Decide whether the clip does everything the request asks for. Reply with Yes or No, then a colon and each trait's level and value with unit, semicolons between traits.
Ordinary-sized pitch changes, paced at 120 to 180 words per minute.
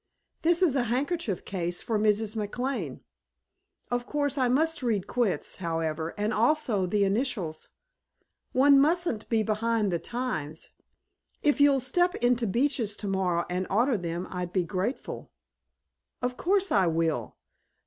No: wide, 6.4 semitones; average, 140 wpm